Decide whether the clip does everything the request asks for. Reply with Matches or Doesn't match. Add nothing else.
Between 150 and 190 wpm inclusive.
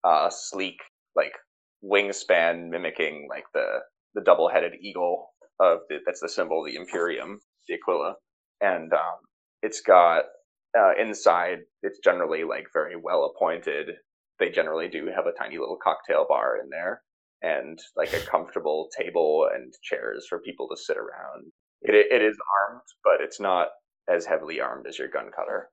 Matches